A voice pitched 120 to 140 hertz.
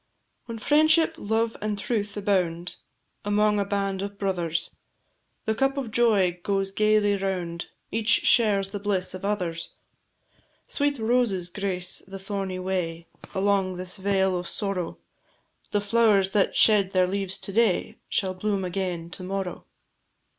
No: high, 195 Hz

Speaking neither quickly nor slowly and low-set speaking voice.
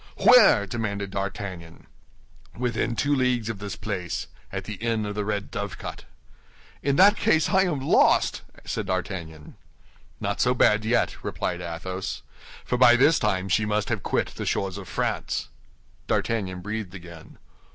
Yes: average, 150 wpm; low, 105 Hz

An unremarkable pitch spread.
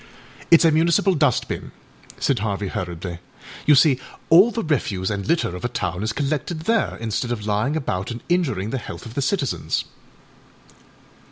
No: wide, 7.5 semitones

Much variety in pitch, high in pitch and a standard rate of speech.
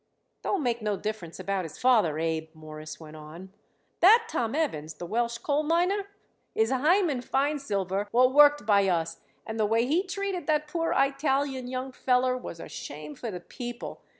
Yes: wide, 8.3 semitones; high, 245 Hz; average, 175 wpm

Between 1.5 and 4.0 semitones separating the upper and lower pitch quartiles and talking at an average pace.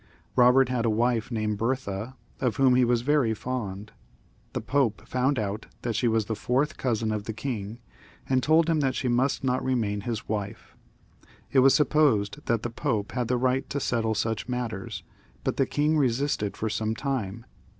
Yes: average, 3.3 semitones; average, 185 wpm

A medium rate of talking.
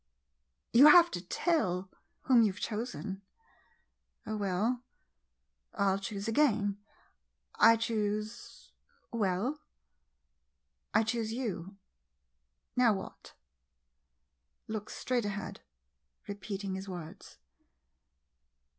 No: slow, 100 wpm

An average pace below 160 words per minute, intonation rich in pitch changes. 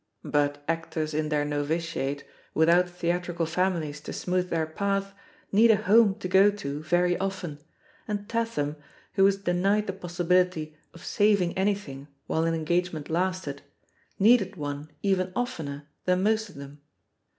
No: average, 150 wpm; average, 4.0 semitones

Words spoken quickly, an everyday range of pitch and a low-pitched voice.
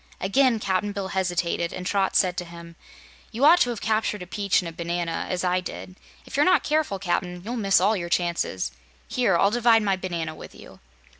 No: fast, 210 wpm; average, 3.8 semitones; high, 190 Hz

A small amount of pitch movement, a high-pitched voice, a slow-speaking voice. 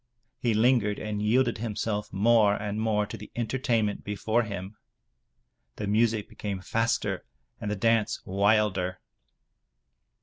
No: narrow, 1.9 semitones; low, 105 Hz; slow, 125 wpm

